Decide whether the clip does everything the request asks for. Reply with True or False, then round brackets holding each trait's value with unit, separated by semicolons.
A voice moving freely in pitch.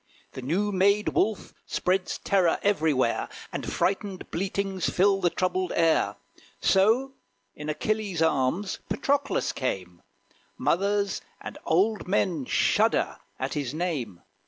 False (4.6 semitones)